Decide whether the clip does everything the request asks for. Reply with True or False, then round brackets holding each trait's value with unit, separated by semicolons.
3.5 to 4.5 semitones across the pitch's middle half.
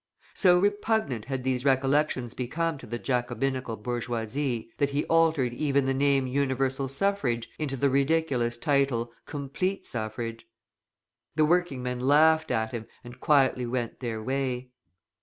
False (3.1 semitones)